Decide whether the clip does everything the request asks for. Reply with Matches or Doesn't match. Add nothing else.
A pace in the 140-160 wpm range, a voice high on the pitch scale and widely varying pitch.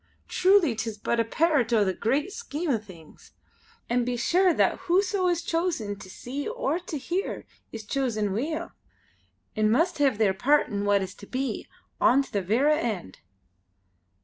Doesn't match